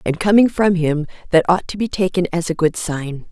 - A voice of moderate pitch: Yes, medium, 175 Hz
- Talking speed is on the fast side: Yes, fast, 235 wpm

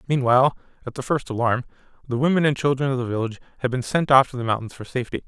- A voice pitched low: Yes, low, 130 Hz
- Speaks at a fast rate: Yes, fast, 240 wpm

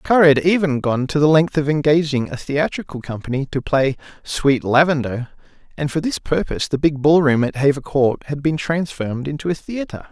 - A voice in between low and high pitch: Yes, medium, 145 Hz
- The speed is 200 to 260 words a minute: No, average, 190 wpm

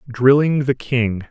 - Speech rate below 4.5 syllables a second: Yes, 4.0 syllables/s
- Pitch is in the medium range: No, low, 130 Hz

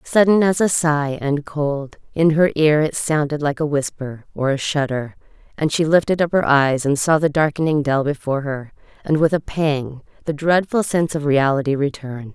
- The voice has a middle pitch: Yes, medium, 150 Hz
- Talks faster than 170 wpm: Yes, average, 195 wpm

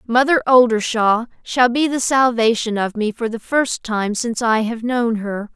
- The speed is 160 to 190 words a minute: Yes, average, 185 wpm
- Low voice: No, high, 235 Hz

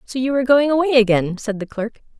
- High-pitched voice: Yes, high, 245 Hz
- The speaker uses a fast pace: Yes, fast, 245 wpm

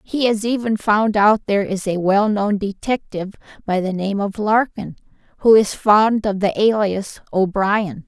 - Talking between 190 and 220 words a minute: No, average, 165 wpm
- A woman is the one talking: Yes, female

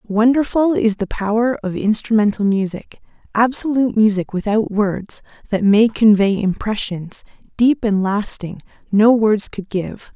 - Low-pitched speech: No, high, 215 Hz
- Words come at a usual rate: No, slow, 130 wpm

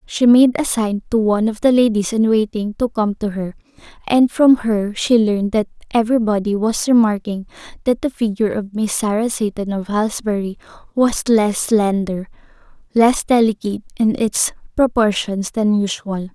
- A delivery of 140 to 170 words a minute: Yes, average, 160 wpm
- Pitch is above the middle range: Yes, high, 215 Hz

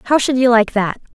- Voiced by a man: No, female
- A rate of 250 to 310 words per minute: Yes, fast, 260 wpm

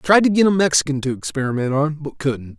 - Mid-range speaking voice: Yes, medium, 150 Hz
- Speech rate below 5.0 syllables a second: No, 6.3 syllables/s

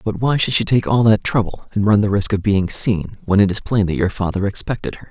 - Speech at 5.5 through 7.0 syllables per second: Yes, 5.8 syllables/s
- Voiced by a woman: No, male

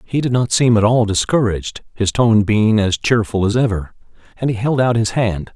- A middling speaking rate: No, fast, 215 wpm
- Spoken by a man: Yes, male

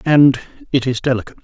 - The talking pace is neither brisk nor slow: Yes, average, 170 wpm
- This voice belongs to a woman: No, male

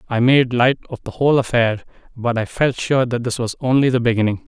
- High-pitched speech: No, low, 120 Hz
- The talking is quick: Yes, fast, 225 wpm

